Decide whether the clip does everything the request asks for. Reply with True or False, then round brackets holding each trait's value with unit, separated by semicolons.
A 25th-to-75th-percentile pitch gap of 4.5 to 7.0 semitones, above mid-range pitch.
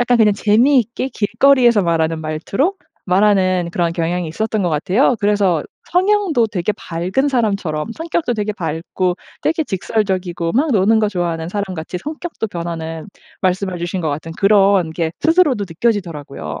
True (5.2 semitones; 195 Hz)